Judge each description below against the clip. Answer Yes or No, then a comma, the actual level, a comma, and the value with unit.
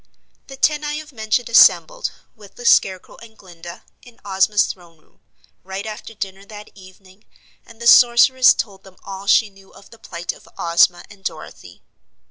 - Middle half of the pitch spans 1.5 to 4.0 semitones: Yes, average, 3.6 semitones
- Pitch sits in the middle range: No, high, 205 Hz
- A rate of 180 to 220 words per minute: No, average, 170 wpm